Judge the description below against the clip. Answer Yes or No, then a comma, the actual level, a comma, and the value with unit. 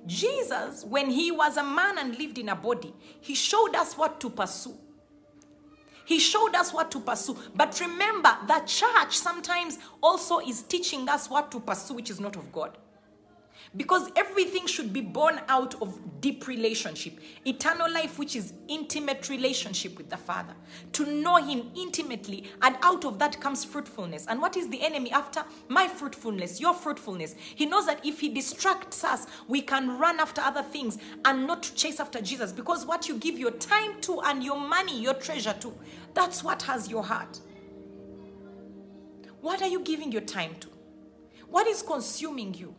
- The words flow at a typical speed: Yes, average, 175 wpm